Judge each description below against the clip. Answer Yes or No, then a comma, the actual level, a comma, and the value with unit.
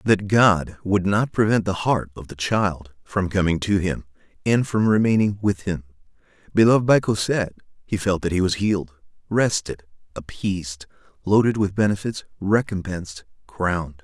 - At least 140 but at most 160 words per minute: Yes, average, 150 wpm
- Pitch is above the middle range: No, very low, 95 Hz